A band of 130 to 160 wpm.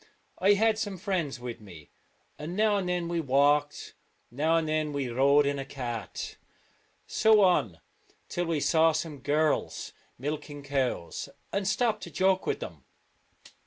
Yes: average, 155 wpm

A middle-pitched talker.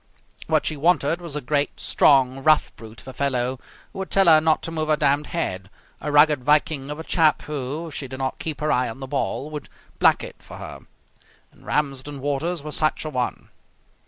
Yes: medium, 145 Hz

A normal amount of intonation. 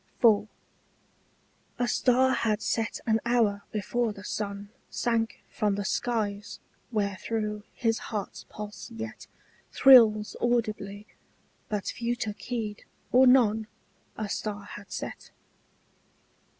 No: narrow, 2.3 semitones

